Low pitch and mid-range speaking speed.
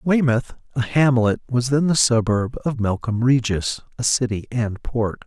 Yes: low, 120 Hz; average, 160 wpm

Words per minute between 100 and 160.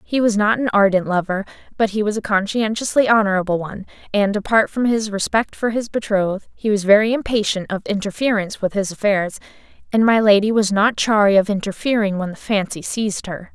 No: average, 190 wpm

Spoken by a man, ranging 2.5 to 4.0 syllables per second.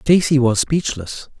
Yes: male; 3.9 syllables/s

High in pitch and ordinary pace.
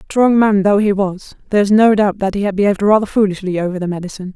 No: high, 200 Hz; fast, 250 wpm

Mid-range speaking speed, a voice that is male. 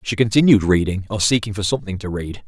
No: fast, 220 wpm; male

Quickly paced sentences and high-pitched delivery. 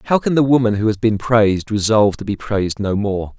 No: fast, 250 wpm; low, 110 Hz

